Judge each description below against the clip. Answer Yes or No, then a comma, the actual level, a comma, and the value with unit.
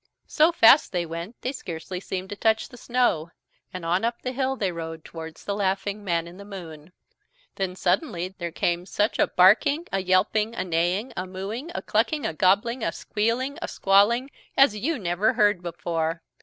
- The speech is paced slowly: No, average, 185 wpm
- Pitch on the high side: Yes, high, 195 Hz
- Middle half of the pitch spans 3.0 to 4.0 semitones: No, average, 4.9 semitones